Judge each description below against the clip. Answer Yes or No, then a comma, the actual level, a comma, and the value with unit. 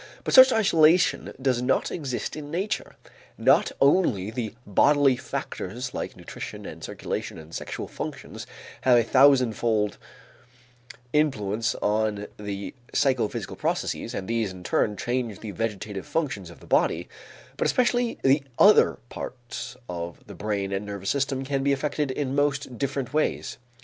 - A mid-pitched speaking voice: No, low, 125 Hz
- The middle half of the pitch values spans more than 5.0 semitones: Yes, wide, 5.5 semitones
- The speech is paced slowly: No, average, 145 wpm